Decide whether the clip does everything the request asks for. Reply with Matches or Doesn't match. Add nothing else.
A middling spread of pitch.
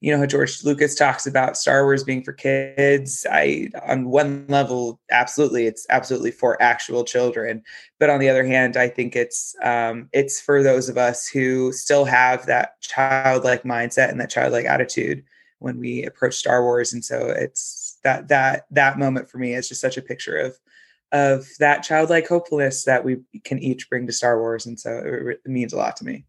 Doesn't match